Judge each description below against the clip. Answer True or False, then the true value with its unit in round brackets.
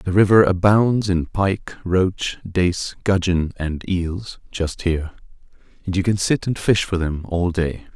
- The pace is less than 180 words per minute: True (165 wpm)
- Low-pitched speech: True (90 Hz)